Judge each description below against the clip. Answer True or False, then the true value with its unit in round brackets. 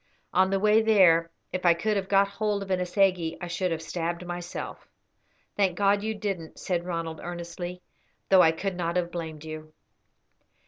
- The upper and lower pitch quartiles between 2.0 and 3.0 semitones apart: True (2.6 semitones)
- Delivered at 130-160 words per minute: False (180 wpm)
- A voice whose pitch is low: False (180 Hz)